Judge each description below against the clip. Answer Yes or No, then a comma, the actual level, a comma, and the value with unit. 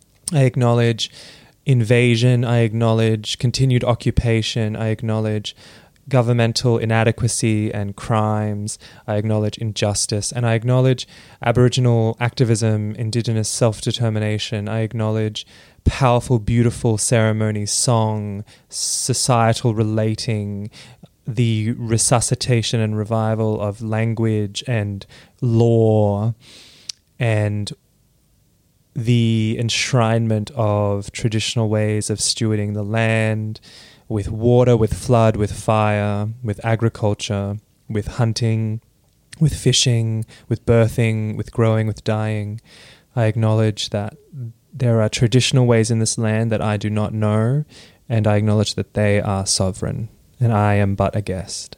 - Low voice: Yes, low, 110 Hz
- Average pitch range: No, narrow, 2.0 semitones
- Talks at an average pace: No, slow, 110 wpm